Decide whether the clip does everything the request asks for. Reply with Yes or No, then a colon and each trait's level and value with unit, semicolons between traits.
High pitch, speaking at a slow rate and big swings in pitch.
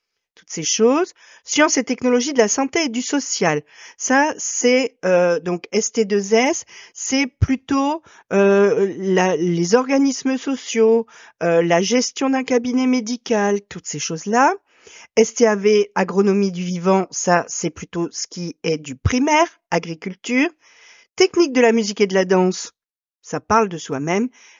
Yes: high, 230 Hz; slow, 140 wpm; wide, 6.8 semitones